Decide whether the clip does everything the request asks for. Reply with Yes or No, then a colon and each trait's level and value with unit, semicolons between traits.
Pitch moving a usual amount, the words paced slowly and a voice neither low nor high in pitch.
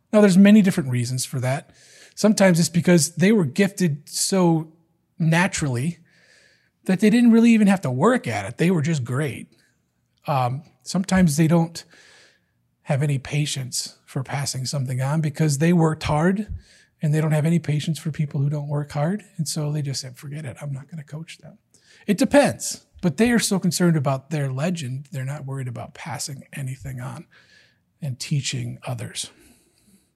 No: average, 4.5 semitones; average, 175 wpm; medium, 155 Hz